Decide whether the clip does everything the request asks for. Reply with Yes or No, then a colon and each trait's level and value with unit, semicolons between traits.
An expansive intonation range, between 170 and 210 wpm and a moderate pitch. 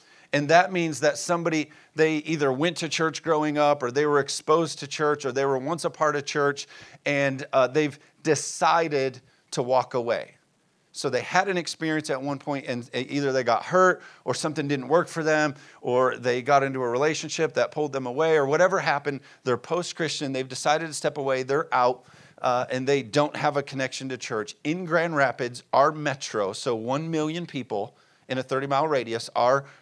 No: average, 2.8 semitones; average, 200 wpm; medium, 145 Hz